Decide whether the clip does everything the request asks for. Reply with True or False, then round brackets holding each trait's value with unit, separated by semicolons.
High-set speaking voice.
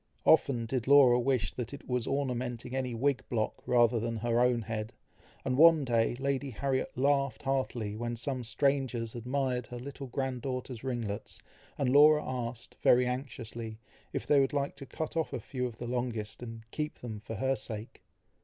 False (125 Hz)